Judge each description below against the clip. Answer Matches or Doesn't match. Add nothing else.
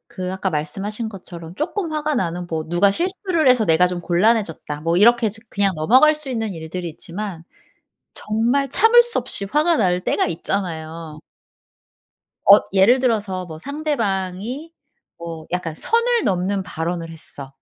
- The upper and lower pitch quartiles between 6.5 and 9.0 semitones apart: Matches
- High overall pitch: Matches